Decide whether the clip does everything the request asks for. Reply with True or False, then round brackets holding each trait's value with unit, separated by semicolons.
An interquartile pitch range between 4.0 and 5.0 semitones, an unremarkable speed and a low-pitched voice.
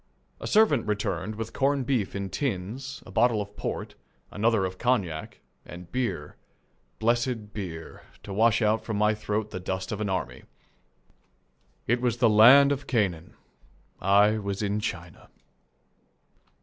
False (3.5 semitones; 145 wpm; 105 Hz)